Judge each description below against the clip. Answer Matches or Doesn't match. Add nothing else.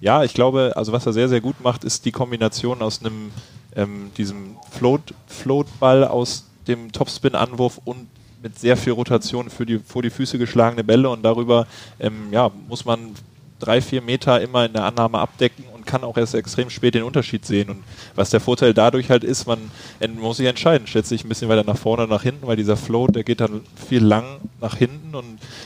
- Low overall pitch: Matches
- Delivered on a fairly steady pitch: Matches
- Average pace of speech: Doesn't match